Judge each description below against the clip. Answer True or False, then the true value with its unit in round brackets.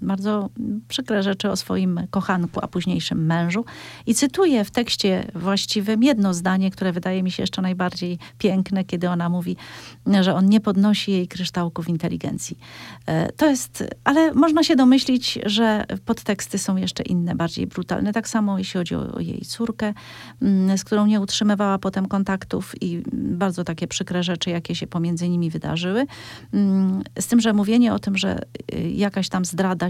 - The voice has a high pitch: True (195 Hz)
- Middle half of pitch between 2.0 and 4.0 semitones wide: True (2.8 semitones)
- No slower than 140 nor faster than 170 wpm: True (160 wpm)